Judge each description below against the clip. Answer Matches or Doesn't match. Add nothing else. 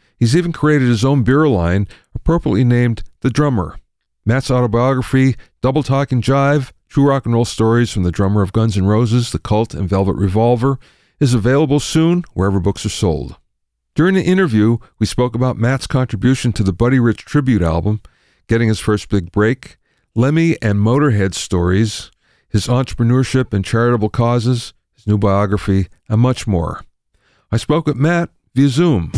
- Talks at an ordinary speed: Matches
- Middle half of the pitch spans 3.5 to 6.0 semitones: Matches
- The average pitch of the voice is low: Matches